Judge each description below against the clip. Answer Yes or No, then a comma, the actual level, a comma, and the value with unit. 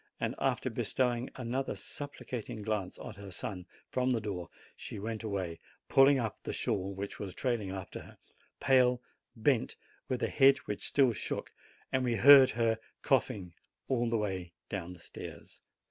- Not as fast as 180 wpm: Yes, average, 160 wpm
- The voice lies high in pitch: No, low, 115 Hz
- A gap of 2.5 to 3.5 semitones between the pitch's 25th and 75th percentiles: No, average, 4.5 semitones